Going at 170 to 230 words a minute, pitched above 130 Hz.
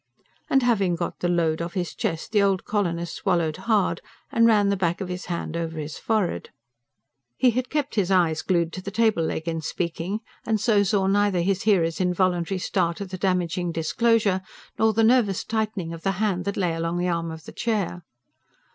Yes: average, 200 wpm; medium, 185 Hz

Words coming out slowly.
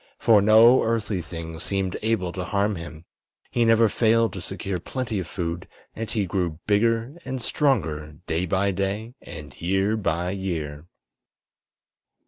No: average, 145 wpm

